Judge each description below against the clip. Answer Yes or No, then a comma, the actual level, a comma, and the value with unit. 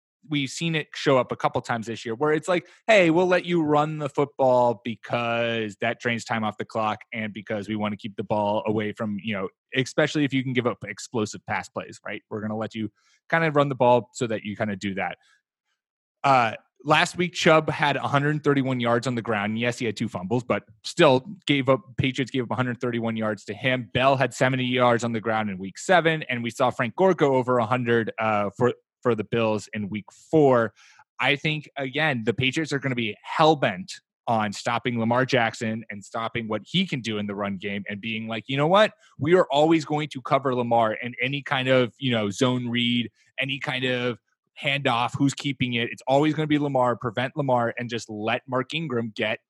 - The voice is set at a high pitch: No, low, 125 Hz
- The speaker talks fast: Yes, fast, 225 wpm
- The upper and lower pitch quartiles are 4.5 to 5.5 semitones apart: No, average, 4.0 semitones